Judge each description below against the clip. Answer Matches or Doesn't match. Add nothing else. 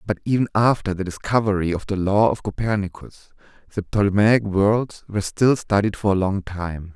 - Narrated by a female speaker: Doesn't match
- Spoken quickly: Doesn't match